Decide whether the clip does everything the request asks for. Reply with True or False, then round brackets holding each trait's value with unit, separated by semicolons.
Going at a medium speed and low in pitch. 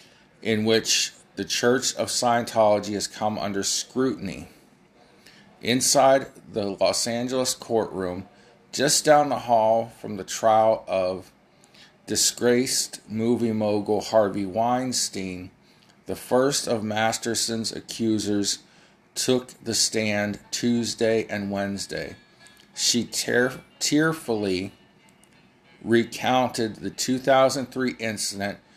False (95 wpm; 110 Hz)